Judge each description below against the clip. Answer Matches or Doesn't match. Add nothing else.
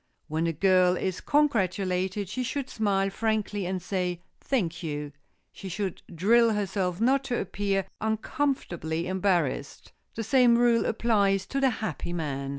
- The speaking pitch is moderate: Doesn't match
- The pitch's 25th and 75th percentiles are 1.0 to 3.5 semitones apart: Doesn't match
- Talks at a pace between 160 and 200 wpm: Doesn't match